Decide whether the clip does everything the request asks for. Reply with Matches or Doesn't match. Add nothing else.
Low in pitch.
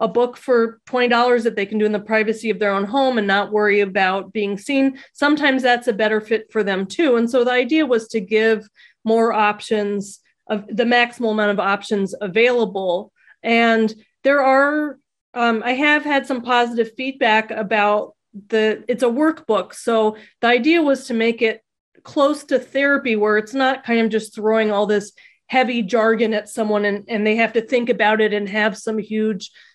Doesn't match